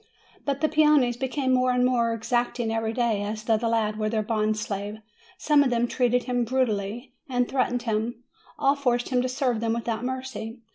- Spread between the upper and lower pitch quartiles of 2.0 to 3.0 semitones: Yes, narrow, 2.4 semitones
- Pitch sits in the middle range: No, high, 240 Hz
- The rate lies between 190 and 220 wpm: Yes, average, 195 wpm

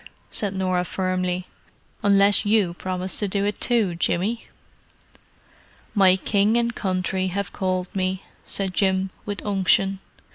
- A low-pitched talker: No, high, 190 Hz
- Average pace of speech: No, slow, 130 wpm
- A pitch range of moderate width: No, narrow, 1.7 semitones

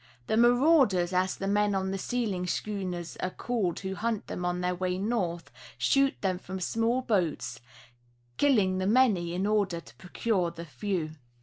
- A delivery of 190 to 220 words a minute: No, average, 170 wpm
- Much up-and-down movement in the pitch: No, average, 3.9 semitones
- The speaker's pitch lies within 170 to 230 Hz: Yes, high, 190 Hz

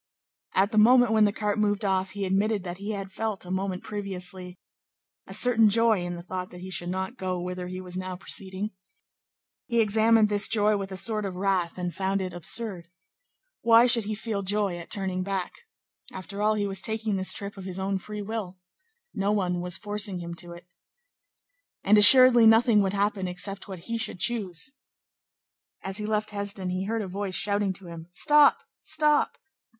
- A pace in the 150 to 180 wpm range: No, average, 195 wpm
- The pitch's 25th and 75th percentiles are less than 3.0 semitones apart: Yes, narrow, 2.5 semitones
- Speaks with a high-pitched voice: Yes, high, 200 Hz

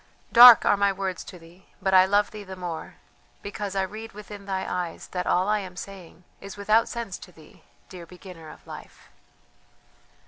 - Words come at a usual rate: Yes, average, 185 wpm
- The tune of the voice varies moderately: No, narrow, 2.1 semitones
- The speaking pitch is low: No, high, 190 Hz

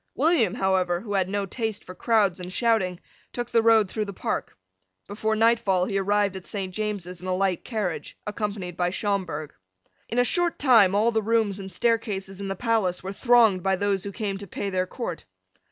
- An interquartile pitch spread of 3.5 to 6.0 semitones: No, average, 3.1 semitones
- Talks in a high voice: Yes, high, 200 Hz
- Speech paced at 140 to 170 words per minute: No, average, 200 wpm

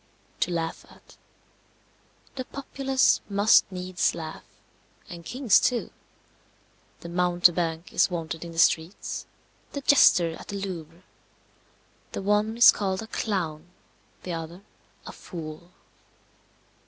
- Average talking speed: No, slow, 115 wpm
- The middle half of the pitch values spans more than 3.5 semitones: Yes, average, 3.9 semitones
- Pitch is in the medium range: Yes, medium, 180 Hz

